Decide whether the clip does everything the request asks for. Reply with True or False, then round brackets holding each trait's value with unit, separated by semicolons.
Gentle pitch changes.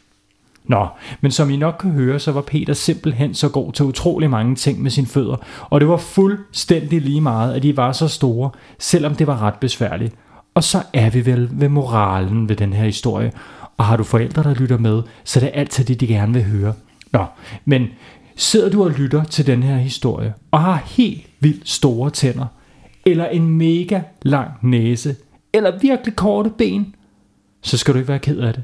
False (4.7 semitones)